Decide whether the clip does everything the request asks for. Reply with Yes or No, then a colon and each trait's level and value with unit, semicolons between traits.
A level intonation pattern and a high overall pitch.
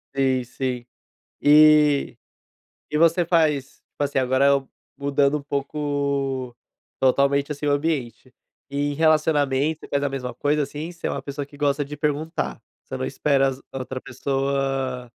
No: narrow, 1.8 semitones; medium, 140 Hz